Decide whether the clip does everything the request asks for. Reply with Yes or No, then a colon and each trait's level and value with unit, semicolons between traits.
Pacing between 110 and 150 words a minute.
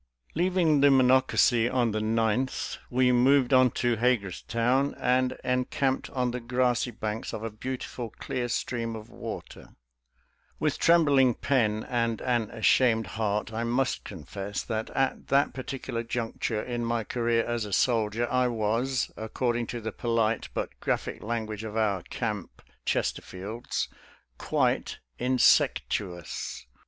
Yes: average, 140 wpm